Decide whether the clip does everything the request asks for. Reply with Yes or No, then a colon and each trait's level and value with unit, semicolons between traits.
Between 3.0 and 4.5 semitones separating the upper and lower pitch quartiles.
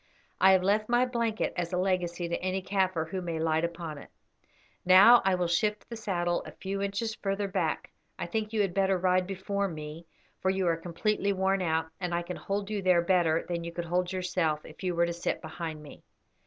No: narrow, 2.4 semitones